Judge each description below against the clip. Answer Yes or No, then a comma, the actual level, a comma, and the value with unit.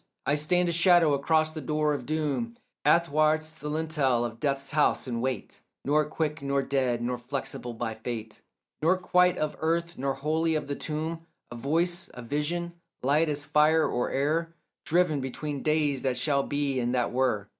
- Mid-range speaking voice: Yes, medium, 150 Hz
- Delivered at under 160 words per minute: No, average, 175 wpm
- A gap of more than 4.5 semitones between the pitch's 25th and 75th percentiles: No, average, 3.3 semitones